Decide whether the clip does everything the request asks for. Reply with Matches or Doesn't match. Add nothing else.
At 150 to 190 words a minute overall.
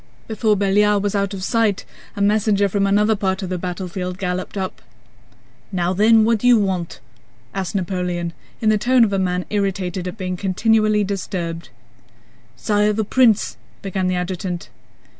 Matches